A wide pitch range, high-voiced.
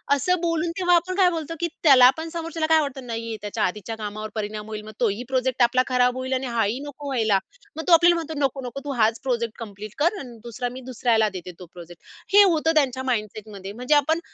Yes: wide, 6.6 semitones; very high, 255 Hz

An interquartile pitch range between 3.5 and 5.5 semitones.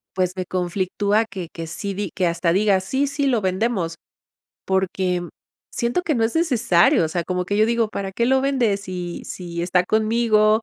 Yes: average, 4.1 semitones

